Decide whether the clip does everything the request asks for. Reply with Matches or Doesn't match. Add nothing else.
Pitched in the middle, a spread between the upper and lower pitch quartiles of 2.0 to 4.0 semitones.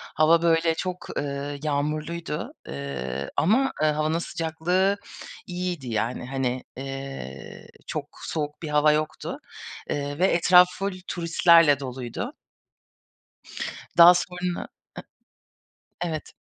Matches